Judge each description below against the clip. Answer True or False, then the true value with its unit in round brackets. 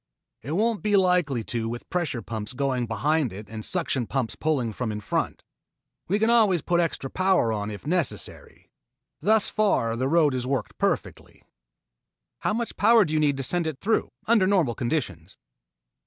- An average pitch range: False (7.9 semitones)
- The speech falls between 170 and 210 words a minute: True (175 wpm)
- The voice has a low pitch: False (145 Hz)